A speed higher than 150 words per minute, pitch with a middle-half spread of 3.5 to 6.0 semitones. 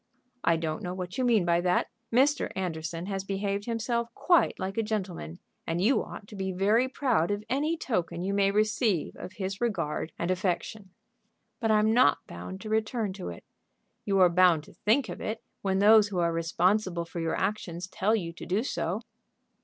Yes: average, 190 wpm; average, 3.8 semitones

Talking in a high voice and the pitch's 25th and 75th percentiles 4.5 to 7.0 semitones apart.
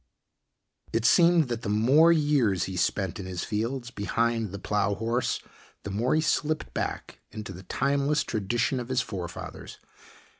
No: low, 115 Hz; average, 5.2 semitones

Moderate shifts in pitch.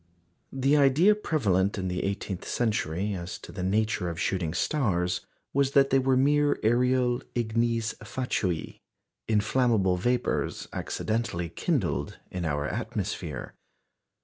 No: wide, 6.2 semitones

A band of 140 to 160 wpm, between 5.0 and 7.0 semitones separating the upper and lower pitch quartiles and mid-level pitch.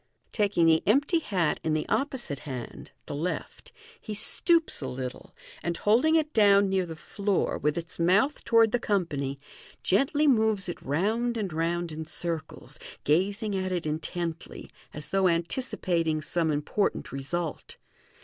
Yes: average, 150 wpm; average, 5.3 semitones; medium, 180 Hz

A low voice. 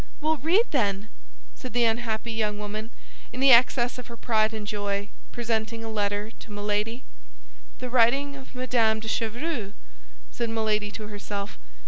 No: high, 225 Hz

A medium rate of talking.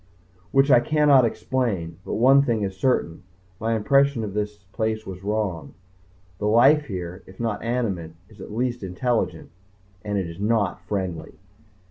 Yes: average, 160 wpm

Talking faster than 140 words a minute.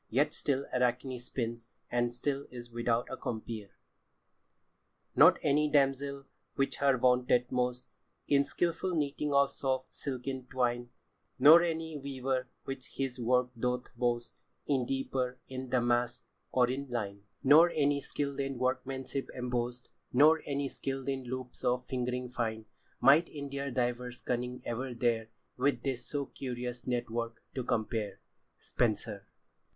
No: slow, 135 wpm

